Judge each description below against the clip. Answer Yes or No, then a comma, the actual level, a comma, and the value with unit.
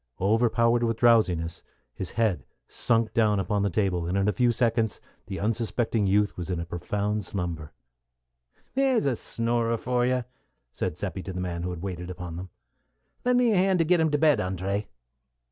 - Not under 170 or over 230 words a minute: Yes, average, 185 wpm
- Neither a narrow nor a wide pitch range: Yes, average, 4.6 semitones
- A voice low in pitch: Yes, low, 105 Hz